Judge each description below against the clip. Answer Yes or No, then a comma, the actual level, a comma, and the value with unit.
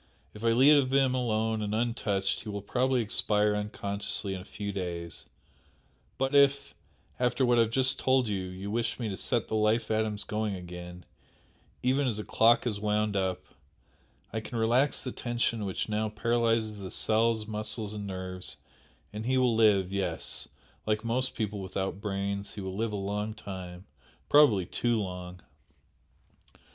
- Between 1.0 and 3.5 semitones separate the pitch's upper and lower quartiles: Yes, average, 2.9 semitones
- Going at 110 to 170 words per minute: Yes, average, 165 wpm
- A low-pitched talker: Yes, low, 105 Hz